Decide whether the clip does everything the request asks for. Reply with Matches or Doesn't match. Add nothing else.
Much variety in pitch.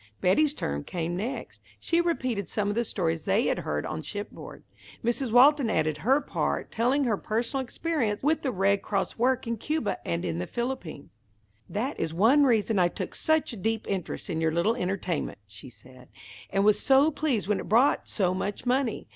Matches